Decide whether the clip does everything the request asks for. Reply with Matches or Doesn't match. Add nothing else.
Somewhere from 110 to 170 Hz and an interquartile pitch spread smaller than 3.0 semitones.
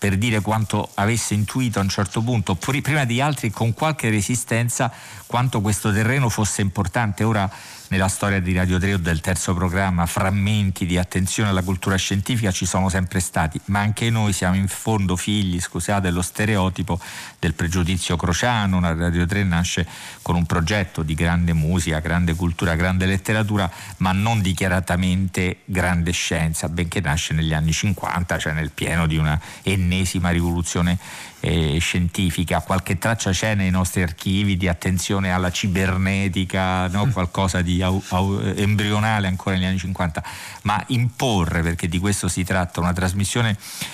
Doesn't match